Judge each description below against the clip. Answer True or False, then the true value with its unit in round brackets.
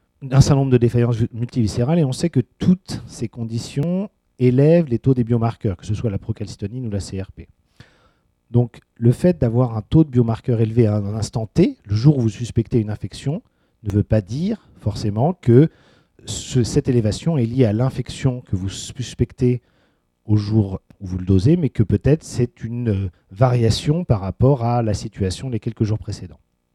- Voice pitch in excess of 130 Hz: False (120 Hz)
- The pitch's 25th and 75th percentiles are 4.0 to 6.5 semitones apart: False (3.6 semitones)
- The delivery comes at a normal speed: True (185 wpm)